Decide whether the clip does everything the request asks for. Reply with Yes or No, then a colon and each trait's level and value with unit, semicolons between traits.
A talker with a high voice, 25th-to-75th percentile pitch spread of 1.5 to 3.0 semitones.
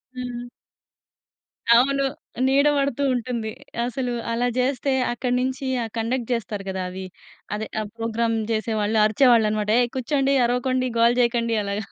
Yes: high, 240 Hz; narrow, 2.5 semitones